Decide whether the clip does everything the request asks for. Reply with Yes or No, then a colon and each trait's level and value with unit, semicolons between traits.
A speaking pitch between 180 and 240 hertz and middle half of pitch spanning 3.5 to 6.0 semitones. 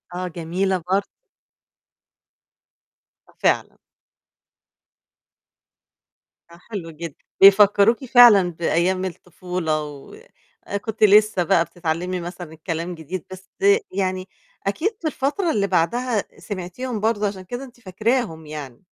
Yes: medium, 185 Hz; average, 4.1 semitones